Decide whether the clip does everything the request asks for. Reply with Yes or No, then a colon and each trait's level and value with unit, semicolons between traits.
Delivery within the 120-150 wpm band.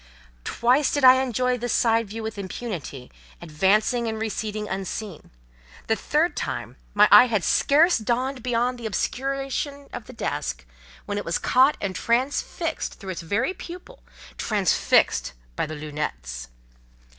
Yes: average, 140 wpm